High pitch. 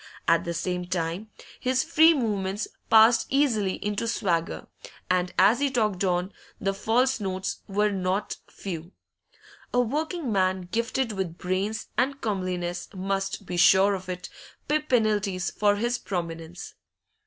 Yes: high, 195 Hz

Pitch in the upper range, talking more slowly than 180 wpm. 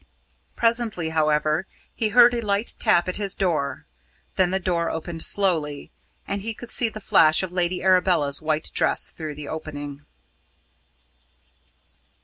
No: medium, 175 Hz; average, 140 wpm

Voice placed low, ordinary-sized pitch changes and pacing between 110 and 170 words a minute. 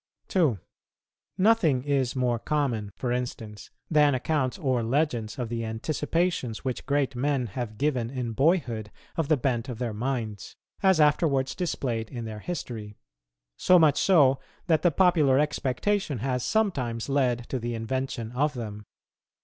Yes: low, 130 Hz; average, 4.2 semitones; average, 150 wpm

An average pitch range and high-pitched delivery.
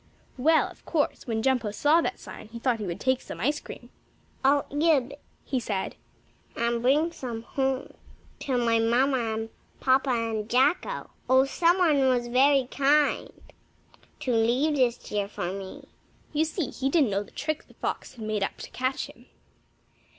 Yes: average, 3.8 semitones; very high, 255 Hz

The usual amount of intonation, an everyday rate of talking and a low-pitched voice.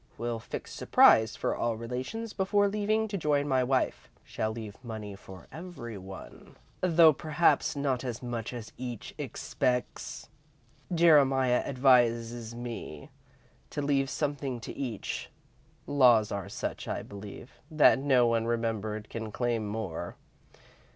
No: average, 4.2 semitones; slow, 130 wpm; low, 125 Hz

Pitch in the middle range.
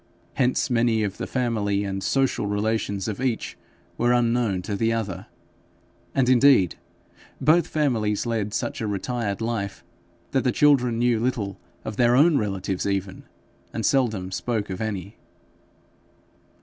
No: low, 110 Hz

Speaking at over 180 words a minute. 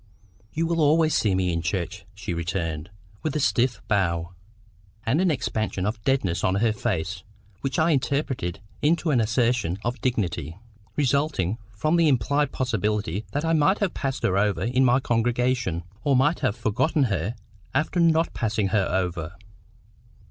No: average, 160 wpm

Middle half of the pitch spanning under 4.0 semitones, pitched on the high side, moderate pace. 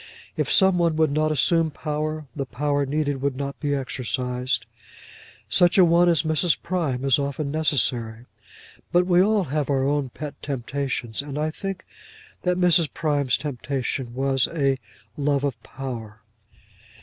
No: average, 3.0 semitones; medium, 145 Hz; average, 150 wpm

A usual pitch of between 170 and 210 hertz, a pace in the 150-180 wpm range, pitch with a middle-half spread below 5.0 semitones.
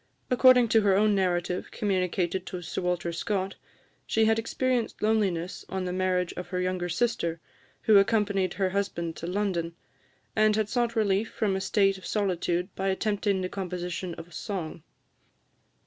Yes: high, 190 Hz; average, 160 wpm; average, 2.9 semitones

